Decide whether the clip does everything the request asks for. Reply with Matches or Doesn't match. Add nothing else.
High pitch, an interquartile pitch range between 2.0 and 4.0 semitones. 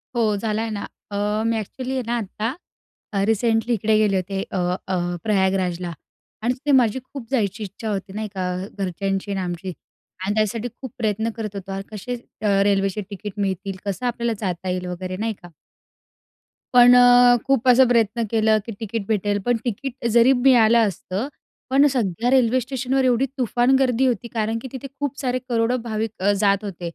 Matches